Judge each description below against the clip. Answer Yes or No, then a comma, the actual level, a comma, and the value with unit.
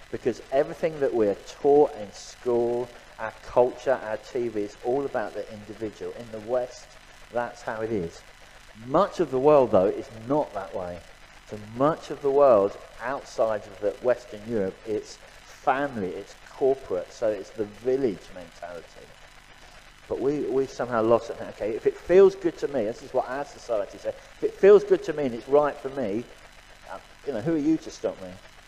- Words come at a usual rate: Yes, average, 185 wpm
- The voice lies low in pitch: No, medium, 150 Hz